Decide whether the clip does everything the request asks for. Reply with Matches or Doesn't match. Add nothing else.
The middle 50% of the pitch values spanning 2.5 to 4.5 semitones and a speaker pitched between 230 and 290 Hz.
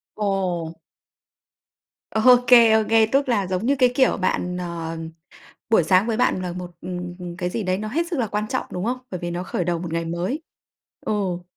Doesn't match